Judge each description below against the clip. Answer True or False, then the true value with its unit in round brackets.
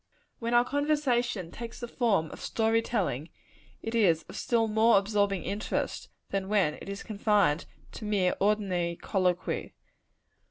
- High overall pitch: True (210 Hz)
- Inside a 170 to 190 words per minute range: False (145 wpm)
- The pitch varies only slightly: False (3.6 semitones)